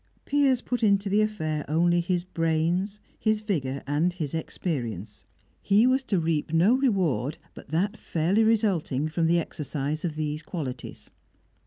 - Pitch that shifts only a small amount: No, average, 5.0 semitones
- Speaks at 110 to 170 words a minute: Yes, average, 150 wpm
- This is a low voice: No, medium, 170 Hz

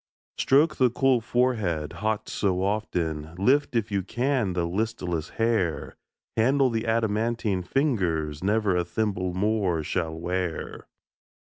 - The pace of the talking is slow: Yes, slow, 125 wpm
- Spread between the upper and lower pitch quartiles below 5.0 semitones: Yes, average, 4.6 semitones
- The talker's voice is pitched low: Yes, low, 105 Hz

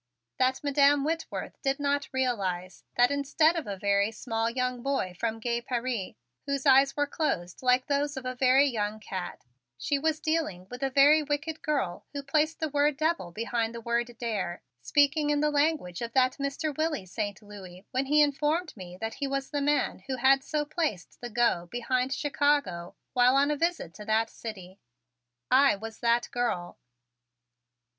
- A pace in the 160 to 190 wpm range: Yes, average, 180 wpm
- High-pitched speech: Yes, very high, 260 Hz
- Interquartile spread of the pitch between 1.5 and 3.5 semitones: No, average, 4.6 semitones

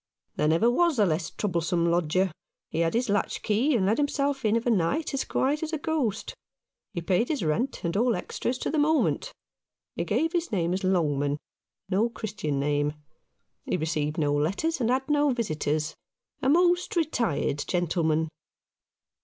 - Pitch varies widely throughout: Yes, wide, 8.9 semitones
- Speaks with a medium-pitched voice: No, high, 205 Hz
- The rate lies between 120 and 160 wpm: No, average, 180 wpm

